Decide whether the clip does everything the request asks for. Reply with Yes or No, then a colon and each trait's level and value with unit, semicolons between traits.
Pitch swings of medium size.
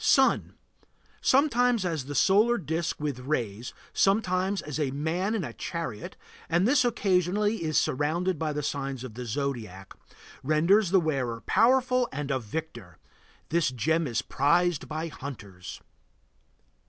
No: wide, 6.1 semitones